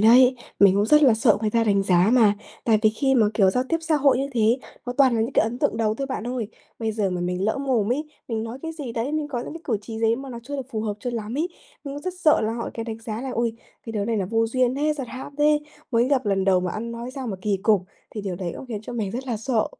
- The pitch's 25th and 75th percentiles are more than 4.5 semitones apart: No, average, 3.7 semitones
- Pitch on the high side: Yes, high, 230 Hz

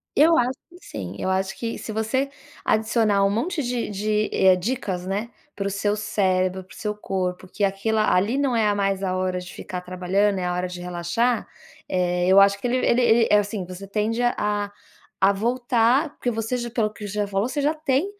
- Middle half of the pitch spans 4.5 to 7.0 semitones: No, average, 3.9 semitones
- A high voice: Yes, high, 205 Hz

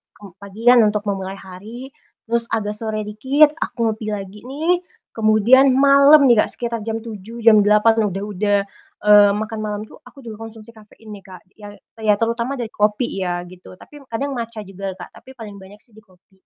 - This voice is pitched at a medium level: No, high, 215 Hz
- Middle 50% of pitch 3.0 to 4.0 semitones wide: No, narrow, 2.4 semitones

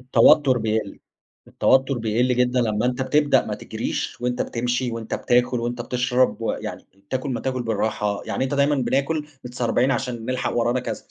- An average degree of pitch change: No, narrow, 2.0 semitones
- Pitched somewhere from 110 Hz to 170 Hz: Yes, low, 125 Hz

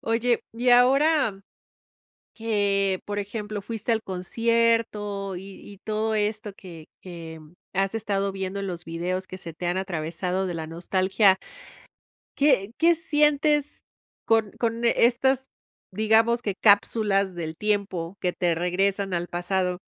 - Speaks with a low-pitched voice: No, high, 200 Hz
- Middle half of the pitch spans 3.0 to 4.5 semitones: Yes, average, 3.6 semitones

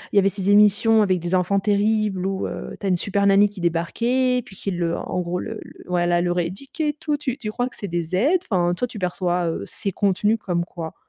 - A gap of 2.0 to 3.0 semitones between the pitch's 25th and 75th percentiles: No, average, 3.5 semitones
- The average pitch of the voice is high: Yes, high, 195 Hz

